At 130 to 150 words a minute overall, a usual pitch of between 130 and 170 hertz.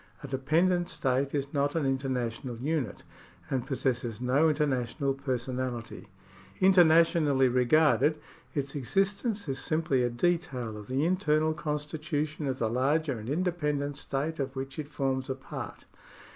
Yes: average, 140 wpm; medium, 140 Hz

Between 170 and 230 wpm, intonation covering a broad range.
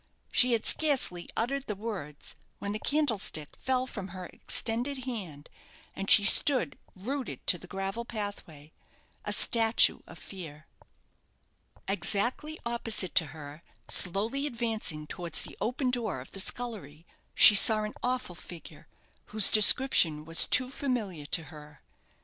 No: average, 140 wpm; wide, 6.3 semitones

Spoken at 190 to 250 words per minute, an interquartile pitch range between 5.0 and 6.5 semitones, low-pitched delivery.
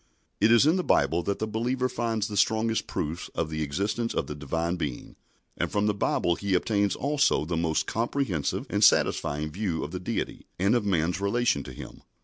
Yes: average, 200 wpm; wide, 5.4 semitones; low, 100 Hz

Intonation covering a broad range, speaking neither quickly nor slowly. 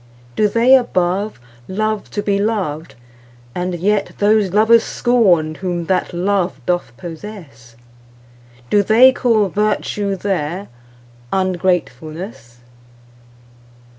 No: wide, 6.0 semitones; slow, 85 wpm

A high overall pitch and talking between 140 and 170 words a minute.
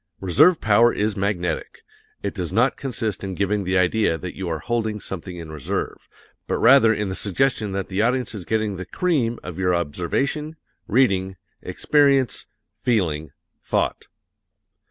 No: low, 100 Hz; average, 155 wpm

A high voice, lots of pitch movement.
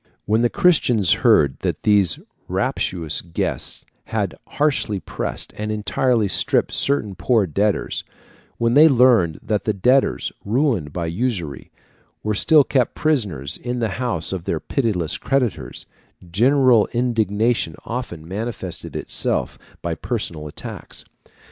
No: low, 110 Hz; wide, 5.7 semitones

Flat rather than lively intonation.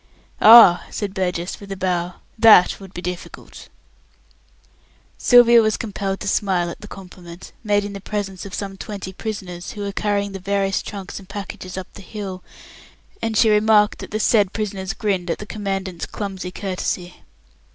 Yes: narrow, 2.2 semitones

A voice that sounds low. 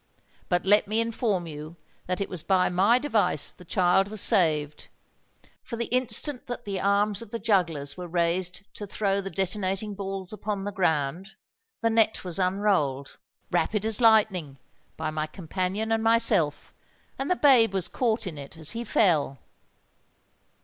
No: high, 195 Hz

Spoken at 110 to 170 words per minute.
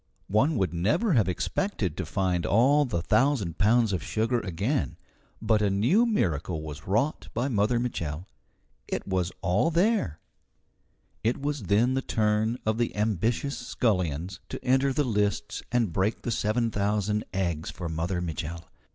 Yes: average, 155 wpm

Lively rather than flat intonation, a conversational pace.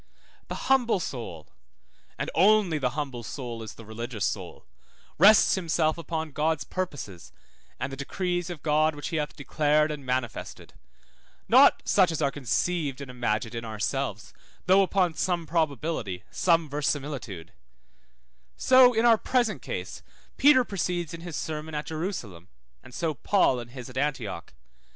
Yes: wide, 5.7 semitones; average, 150 wpm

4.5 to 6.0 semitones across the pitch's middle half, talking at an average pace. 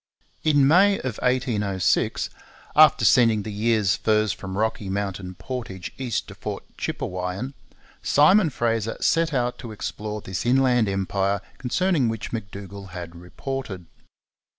No: average, 4.8 semitones; slow, 130 wpm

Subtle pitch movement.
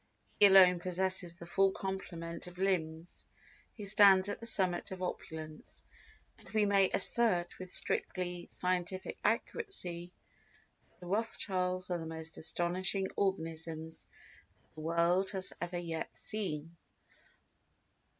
Yes: narrow, 2.2 semitones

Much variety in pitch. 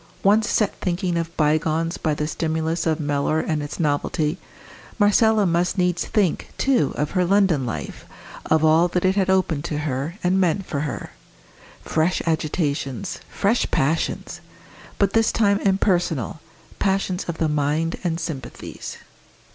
No: average, 3.6 semitones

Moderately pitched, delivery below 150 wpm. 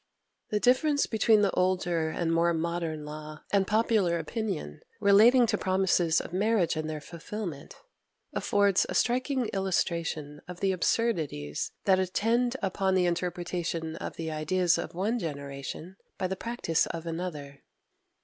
Yes: medium, 180 Hz; average, 140 wpm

